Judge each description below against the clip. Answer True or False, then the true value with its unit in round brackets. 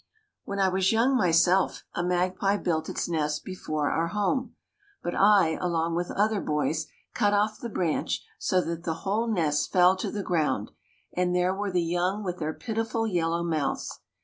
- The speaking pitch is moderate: True (180 Hz)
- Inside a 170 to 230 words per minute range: True (175 wpm)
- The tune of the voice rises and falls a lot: False (3.5 semitones)